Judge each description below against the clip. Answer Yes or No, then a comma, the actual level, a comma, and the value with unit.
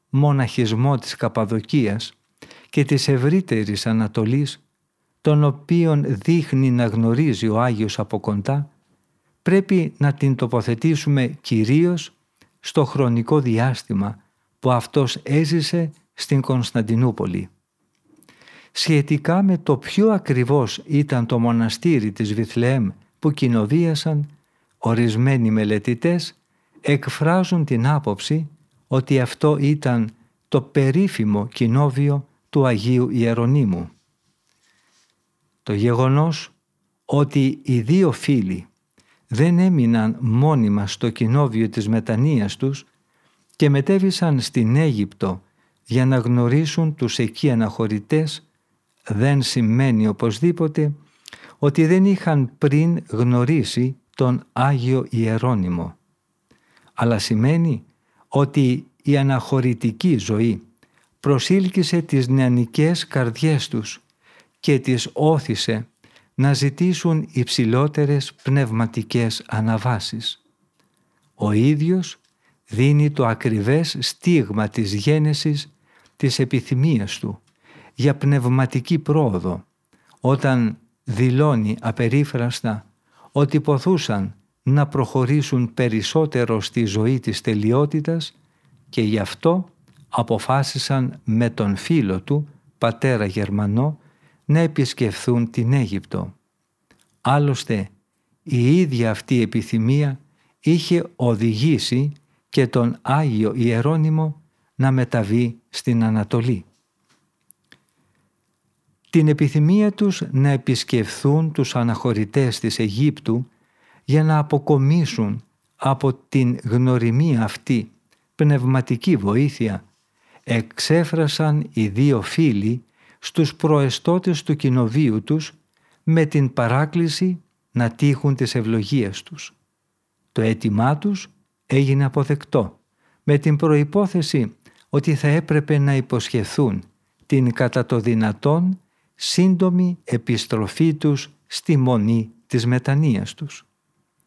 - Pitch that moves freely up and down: No, average, 4.6 semitones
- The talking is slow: Yes, slow, 95 wpm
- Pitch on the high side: No, low, 135 Hz